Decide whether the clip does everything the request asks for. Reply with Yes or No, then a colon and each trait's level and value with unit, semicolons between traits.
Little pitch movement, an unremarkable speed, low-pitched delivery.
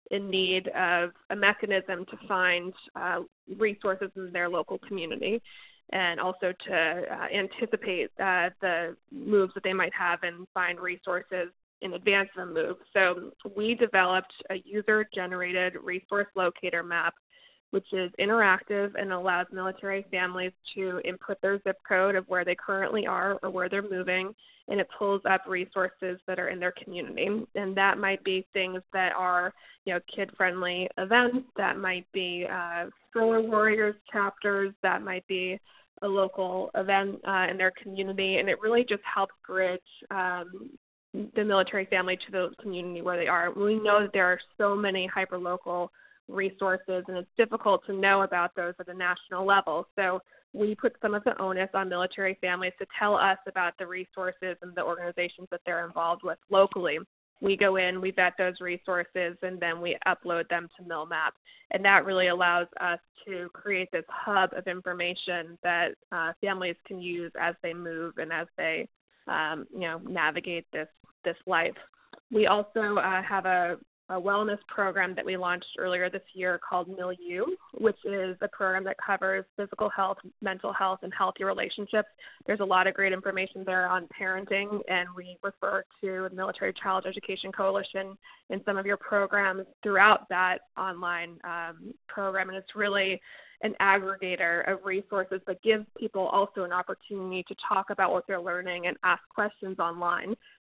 No: narrow, 1.6 semitones; average, 170 wpm; high, 190 Hz